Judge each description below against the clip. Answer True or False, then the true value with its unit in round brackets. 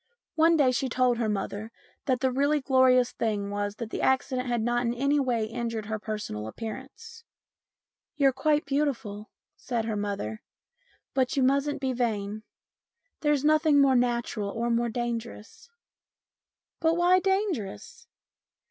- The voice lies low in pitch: False (245 Hz)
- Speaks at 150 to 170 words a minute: True (155 wpm)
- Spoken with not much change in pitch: False (4.1 semitones)